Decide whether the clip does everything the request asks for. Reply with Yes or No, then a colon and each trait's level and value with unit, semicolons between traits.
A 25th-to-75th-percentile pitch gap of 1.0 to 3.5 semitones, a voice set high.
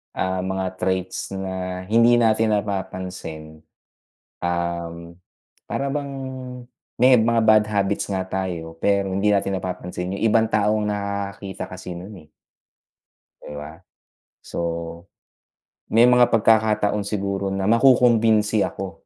No: average, 2.9 semitones; low, 100 Hz